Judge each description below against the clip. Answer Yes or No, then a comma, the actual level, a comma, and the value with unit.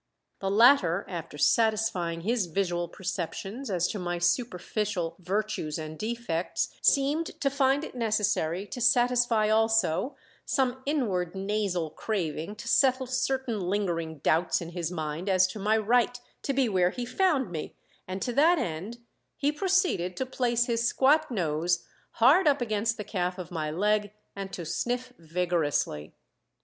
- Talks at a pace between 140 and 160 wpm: Yes, average, 150 wpm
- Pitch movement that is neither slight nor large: No, wide, 5.9 semitones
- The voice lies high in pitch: Yes, high, 205 Hz